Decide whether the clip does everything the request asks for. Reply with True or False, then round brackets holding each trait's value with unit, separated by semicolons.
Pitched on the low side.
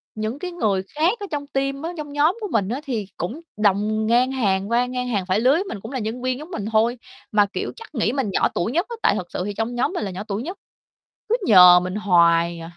False (230 Hz)